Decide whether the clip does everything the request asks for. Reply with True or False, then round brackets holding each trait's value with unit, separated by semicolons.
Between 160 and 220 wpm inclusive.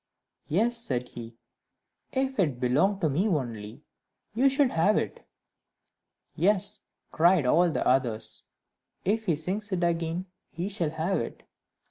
False (135 wpm)